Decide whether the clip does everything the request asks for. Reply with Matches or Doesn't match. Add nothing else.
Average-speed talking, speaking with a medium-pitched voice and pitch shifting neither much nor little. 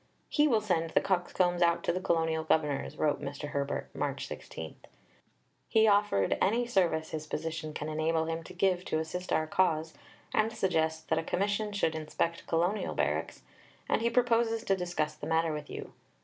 Matches